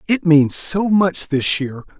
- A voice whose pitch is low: No, medium, 170 Hz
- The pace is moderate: Yes, average, 180 wpm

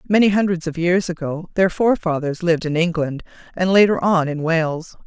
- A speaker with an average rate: Yes, average, 180 wpm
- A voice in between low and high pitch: Yes, medium, 170 Hz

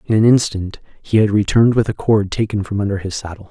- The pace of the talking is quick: Yes, fast, 240 wpm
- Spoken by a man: Yes, male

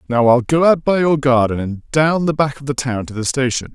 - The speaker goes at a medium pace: No, fast, 275 wpm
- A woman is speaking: No, male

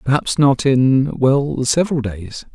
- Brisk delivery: No, slow, 120 wpm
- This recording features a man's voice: Yes, male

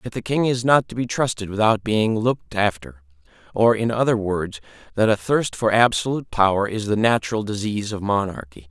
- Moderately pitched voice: No, low, 105 Hz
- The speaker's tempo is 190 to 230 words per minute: Yes, average, 195 wpm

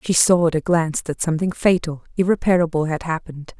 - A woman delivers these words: Yes, female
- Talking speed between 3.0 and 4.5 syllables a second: No, 6.3 syllables/s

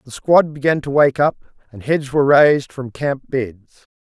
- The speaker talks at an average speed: Yes, average, 195 wpm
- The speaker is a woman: No, male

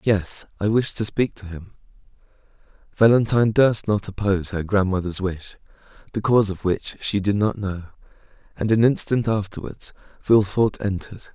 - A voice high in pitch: No, low, 100 Hz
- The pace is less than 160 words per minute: Yes, average, 150 wpm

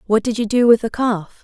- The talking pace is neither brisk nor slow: No, fast, 295 wpm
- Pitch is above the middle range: Yes, high, 225 Hz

